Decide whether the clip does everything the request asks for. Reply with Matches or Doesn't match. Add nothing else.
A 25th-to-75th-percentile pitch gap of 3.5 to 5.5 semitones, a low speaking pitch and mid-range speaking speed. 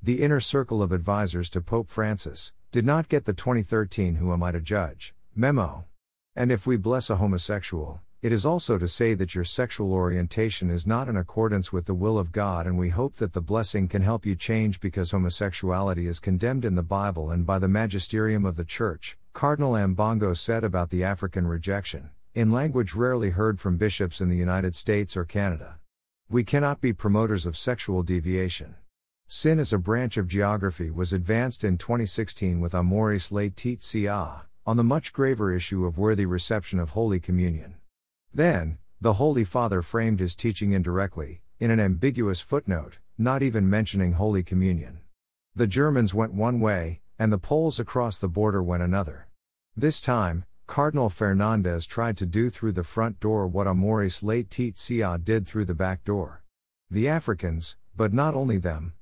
Matches